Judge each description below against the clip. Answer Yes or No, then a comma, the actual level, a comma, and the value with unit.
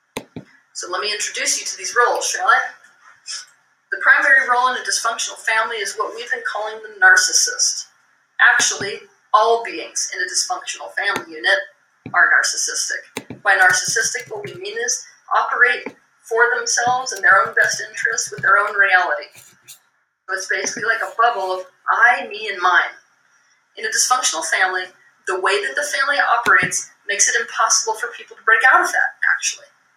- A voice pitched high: Yes, very high, 280 Hz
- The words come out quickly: No, average, 170 wpm